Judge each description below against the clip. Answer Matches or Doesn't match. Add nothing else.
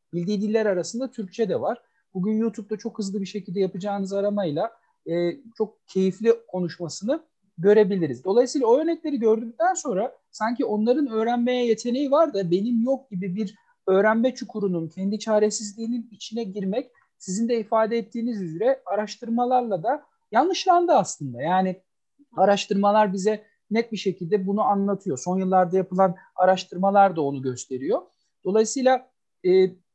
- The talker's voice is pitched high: Matches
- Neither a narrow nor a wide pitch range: Matches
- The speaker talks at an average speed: Matches